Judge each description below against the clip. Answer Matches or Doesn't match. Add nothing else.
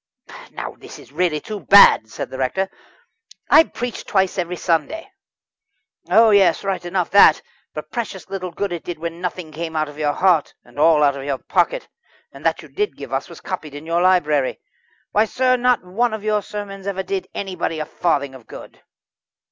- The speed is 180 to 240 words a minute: Matches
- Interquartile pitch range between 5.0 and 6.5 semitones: Doesn't match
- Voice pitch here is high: Doesn't match